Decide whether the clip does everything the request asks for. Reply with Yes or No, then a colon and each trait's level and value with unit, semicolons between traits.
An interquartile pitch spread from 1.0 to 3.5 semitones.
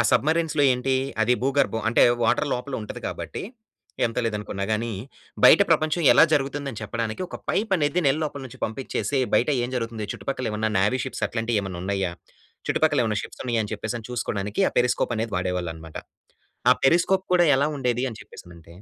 No: average, 4.7 semitones